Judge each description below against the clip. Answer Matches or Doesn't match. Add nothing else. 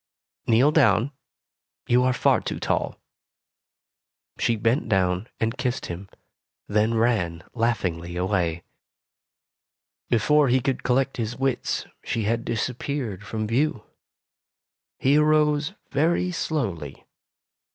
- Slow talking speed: Matches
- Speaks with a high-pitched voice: Doesn't match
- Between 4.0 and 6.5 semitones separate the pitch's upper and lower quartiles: Matches